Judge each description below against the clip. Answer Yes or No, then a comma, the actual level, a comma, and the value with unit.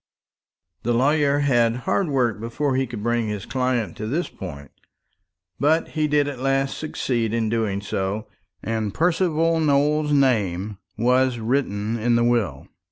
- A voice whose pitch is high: No, low, 120 Hz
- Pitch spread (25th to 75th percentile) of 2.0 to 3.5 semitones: No, average, 4.6 semitones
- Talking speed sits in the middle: Yes, average, 150 wpm